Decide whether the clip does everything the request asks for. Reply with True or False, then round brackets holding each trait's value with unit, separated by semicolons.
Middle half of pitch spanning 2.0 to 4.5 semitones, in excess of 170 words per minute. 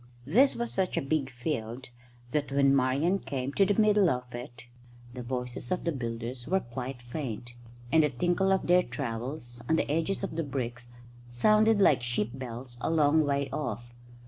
False (5.2 semitones; 180 wpm)